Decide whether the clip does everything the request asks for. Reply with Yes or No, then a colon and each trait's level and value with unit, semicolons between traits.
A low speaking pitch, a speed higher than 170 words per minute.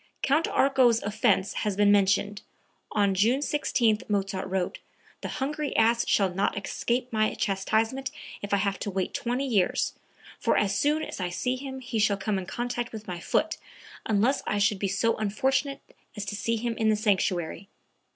No: high, 215 Hz; average, 180 wpm